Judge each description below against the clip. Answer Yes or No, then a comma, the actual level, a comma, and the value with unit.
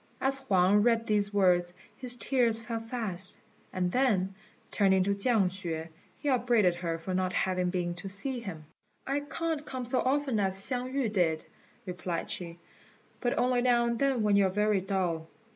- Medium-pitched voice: No, high, 205 Hz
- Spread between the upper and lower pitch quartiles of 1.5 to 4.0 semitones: No, average, 5.1 semitones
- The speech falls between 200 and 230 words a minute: No, average, 175 wpm